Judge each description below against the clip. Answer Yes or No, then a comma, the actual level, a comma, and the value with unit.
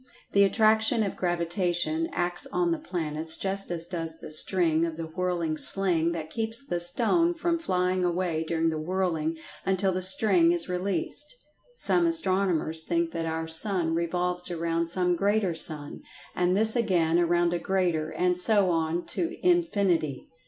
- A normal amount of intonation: Yes, average, 3.1 semitones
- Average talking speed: Yes, average, 160 wpm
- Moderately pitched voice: Yes, medium, 180 Hz